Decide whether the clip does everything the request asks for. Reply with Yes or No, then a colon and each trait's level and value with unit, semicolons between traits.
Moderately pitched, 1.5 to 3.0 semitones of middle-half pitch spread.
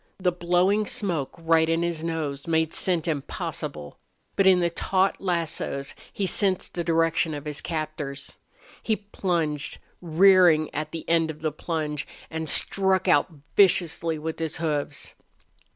Yes: medium, 165 Hz; average, 2.7 semitones